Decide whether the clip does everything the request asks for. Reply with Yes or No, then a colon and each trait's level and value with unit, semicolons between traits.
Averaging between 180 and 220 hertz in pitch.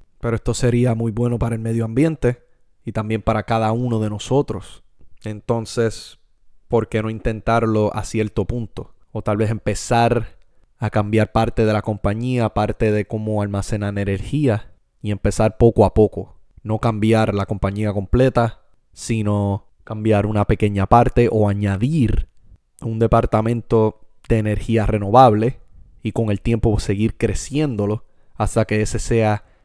No: low, 110 Hz